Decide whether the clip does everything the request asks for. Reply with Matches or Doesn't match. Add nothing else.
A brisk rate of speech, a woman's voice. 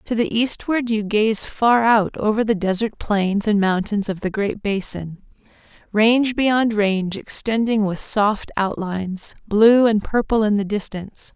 Doesn't match